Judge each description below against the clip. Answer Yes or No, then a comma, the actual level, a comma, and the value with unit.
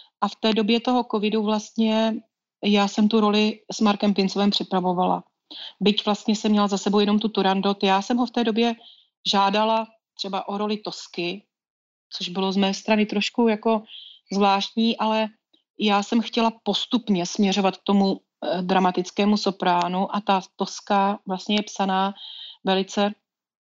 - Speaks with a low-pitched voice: No, high, 205 Hz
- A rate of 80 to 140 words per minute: No, average, 150 wpm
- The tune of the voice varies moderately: No, narrow, 2.1 semitones